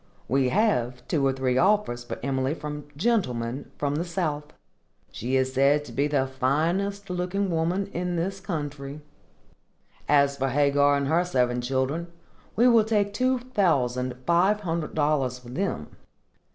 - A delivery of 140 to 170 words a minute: Yes, average, 150 wpm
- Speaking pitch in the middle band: Yes, medium, 145 Hz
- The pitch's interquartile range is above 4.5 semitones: Yes, wide, 5.5 semitones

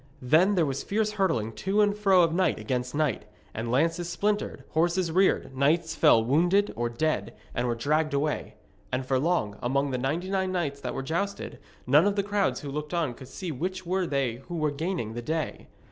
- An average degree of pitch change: No, wide, 5.7 semitones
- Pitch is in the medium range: Yes, medium, 160 Hz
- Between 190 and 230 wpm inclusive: Yes, fast, 205 wpm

